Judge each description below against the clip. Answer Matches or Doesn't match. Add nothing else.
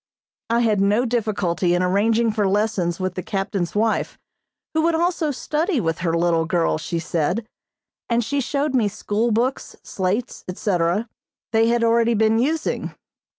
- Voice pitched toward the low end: Doesn't match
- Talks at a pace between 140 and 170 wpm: Matches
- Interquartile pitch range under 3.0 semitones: Doesn't match